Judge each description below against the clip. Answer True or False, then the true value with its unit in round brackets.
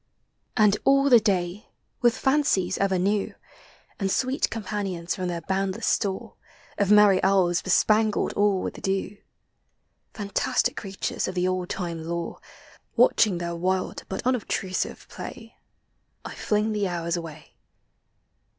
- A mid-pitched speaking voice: False (195 Hz)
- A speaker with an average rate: False (130 wpm)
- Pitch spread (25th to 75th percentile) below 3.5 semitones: True (2.7 semitones)